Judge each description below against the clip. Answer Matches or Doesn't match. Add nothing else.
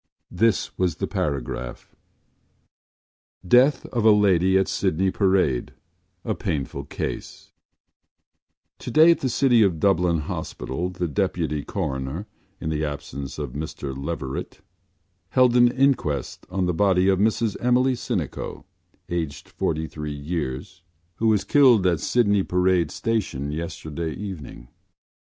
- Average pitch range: Doesn't match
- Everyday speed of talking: Doesn't match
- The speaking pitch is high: Doesn't match